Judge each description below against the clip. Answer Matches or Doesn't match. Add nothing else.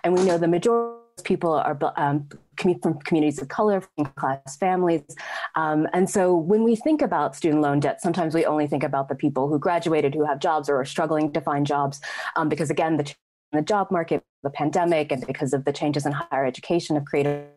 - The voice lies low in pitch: Doesn't match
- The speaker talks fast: Matches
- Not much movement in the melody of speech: Doesn't match